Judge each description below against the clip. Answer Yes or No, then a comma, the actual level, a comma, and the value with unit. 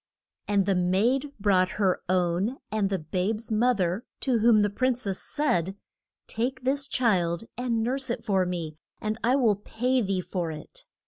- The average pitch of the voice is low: No, high, 210 Hz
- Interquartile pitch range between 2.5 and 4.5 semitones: No, average, 5.0 semitones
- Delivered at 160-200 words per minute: Yes, average, 175 wpm